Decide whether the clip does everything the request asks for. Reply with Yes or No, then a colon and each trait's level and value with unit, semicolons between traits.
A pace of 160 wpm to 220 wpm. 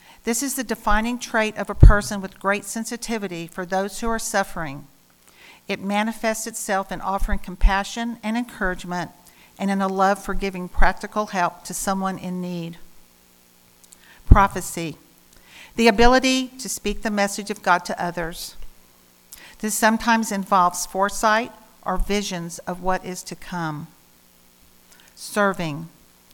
No: slow, 135 wpm